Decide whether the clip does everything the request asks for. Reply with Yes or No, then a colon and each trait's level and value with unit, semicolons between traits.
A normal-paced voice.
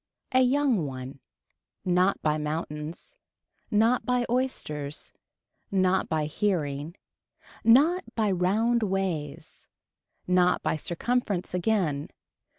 No: slow, 95 wpm